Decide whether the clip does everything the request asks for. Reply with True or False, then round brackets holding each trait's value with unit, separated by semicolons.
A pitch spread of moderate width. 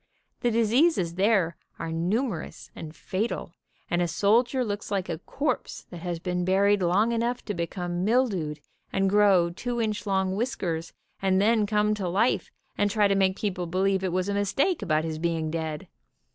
True (3.5 semitones)